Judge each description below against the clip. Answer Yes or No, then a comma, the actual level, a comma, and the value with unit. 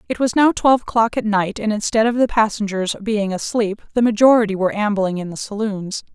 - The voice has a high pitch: Yes, high, 215 Hz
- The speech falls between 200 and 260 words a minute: Yes, fast, 205 wpm